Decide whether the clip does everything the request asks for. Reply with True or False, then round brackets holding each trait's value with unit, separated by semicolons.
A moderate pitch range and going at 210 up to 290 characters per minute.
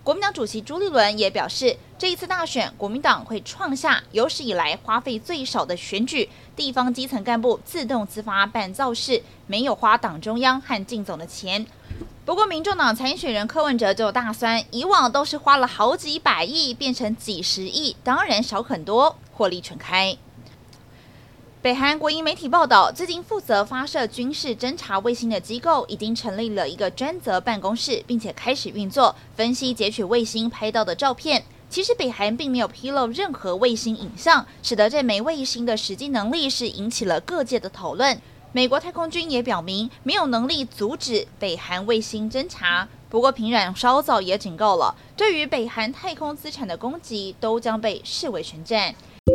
True (4.9 semitones; 280 characters per minute)